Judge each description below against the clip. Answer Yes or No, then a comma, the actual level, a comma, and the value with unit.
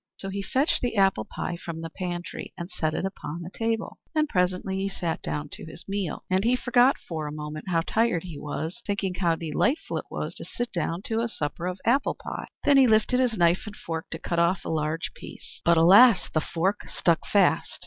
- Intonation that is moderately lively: Yes, average, 5.0 semitones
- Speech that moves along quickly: Yes, fast, 220 wpm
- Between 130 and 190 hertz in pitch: Yes, medium, 185 Hz